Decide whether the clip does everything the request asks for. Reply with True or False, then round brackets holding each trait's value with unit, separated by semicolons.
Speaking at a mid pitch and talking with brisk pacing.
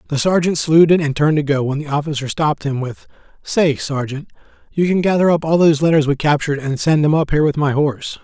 True (150 Hz; 235 wpm)